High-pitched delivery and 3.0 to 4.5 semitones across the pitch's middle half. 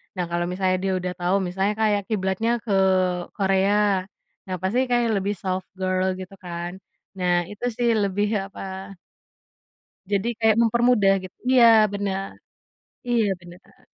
No: high, 195 Hz; narrow, 2.5 semitones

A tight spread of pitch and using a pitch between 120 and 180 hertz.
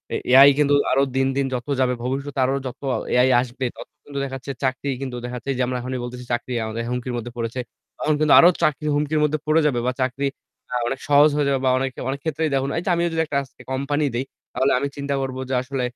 Yes: narrow, 2.2 semitones; low, 135 Hz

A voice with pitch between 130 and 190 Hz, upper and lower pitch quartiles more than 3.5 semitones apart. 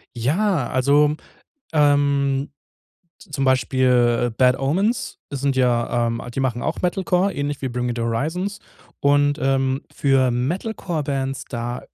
No: low, 135 Hz; average, 2.9 semitones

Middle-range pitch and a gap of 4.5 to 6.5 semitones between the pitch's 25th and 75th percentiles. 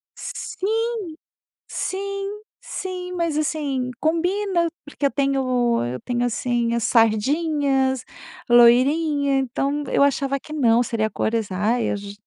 No: very high, 270 Hz; average, 4.8 semitones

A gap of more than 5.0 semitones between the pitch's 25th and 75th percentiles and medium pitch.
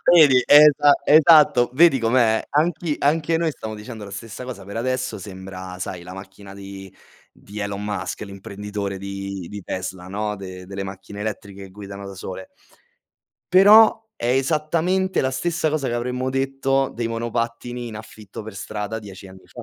No: wide, 5.5 semitones; low, 110 Hz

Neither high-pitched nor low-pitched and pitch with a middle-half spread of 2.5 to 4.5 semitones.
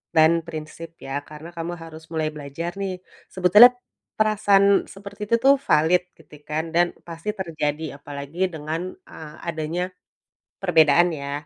Yes: medium, 165 Hz; average, 2.8 semitones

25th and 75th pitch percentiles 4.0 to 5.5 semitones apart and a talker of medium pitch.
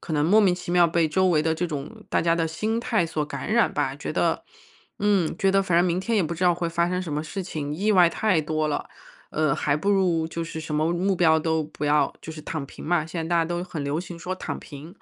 No: average, 2.7 semitones; medium, 170 Hz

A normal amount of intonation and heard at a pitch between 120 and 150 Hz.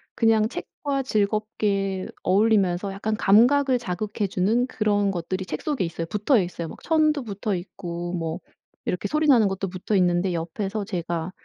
No: average, 3.7 semitones; high, 200 Hz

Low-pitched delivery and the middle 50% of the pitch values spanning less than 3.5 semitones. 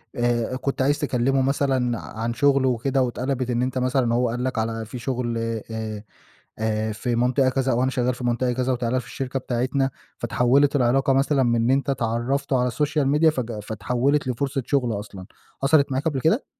Yes: low, 125 Hz; narrow, 2.4 semitones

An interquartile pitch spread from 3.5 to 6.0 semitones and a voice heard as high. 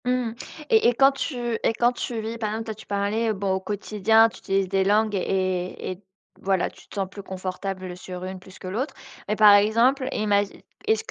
No: average, 2.8 semitones; high, 205 Hz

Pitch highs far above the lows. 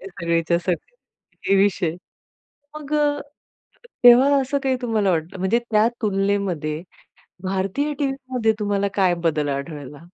Yes: wide, 6.5 semitones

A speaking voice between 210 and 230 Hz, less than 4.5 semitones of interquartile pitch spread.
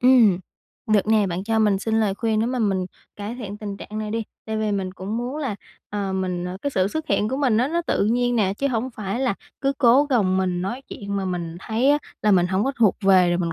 Yes: high, 215 Hz; average, 4.1 semitones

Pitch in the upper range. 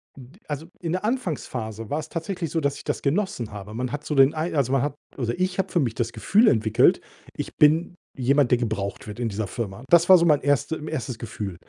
No: medium, 140 Hz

